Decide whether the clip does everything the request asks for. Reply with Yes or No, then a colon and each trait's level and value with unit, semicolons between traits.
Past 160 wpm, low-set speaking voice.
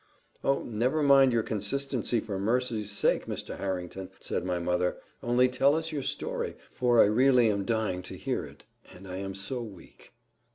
Yes: average, 175 wpm; low, 110 Hz